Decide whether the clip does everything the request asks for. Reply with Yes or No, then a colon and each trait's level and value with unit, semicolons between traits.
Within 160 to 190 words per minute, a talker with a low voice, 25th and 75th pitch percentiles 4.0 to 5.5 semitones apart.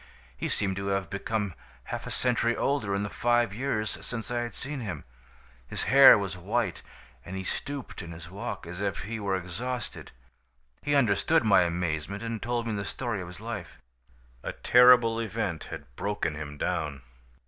Yes: average, 180 wpm; low, 100 Hz; average, 4.7 semitones